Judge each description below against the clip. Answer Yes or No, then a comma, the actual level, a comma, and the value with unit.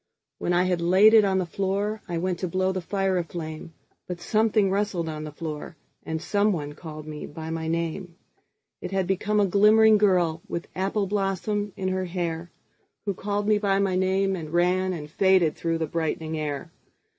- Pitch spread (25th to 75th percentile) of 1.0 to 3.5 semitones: Yes, average, 3.1 semitones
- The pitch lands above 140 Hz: Yes, medium, 185 Hz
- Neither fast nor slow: Yes, average, 170 wpm